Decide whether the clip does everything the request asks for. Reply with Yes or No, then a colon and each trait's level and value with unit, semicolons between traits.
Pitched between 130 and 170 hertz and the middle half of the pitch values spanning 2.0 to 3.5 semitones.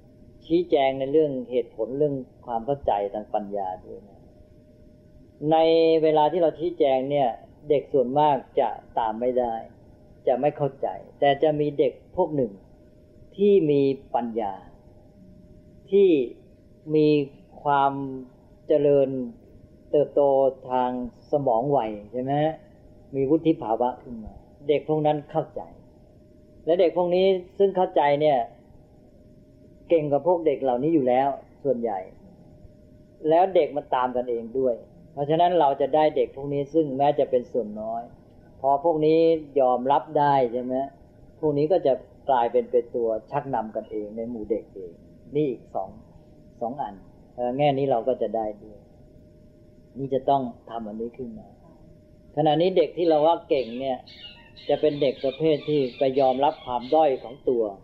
No: low, 135 Hz; average, 4.0 semitones